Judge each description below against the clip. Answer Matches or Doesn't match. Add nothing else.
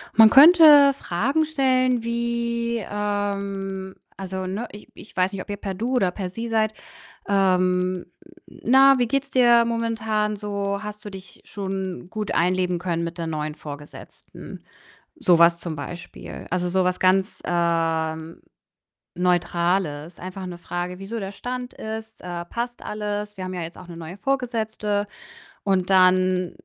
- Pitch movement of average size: Matches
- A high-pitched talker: Matches